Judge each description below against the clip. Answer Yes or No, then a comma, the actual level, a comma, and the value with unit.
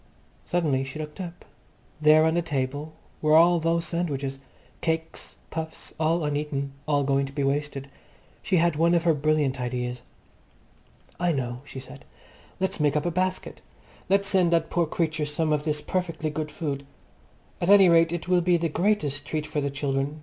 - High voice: No, medium, 155 Hz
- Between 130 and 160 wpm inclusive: No, average, 180 wpm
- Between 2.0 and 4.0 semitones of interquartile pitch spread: Yes, average, 2.9 semitones